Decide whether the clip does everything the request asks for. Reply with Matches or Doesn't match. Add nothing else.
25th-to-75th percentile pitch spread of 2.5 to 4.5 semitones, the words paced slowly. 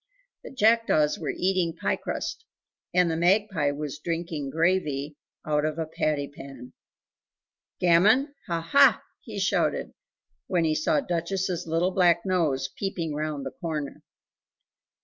Matches